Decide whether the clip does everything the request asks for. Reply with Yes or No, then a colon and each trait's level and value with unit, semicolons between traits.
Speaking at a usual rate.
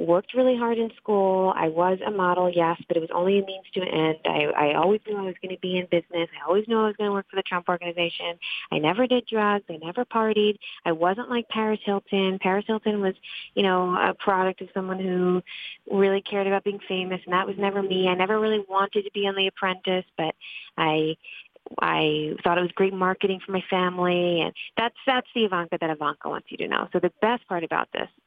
No: fast, 230 wpm